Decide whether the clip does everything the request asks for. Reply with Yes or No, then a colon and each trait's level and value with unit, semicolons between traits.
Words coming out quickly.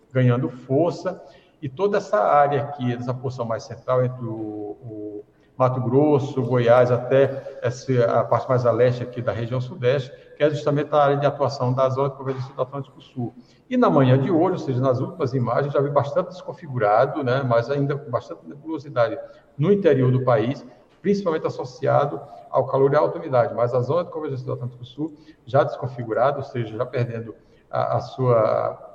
Yes: fast, 190 wpm